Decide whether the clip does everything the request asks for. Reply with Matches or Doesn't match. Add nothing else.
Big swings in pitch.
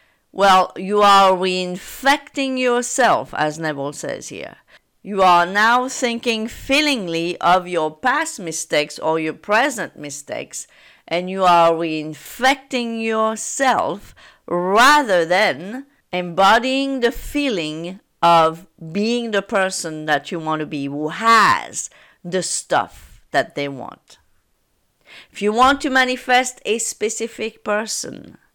Matches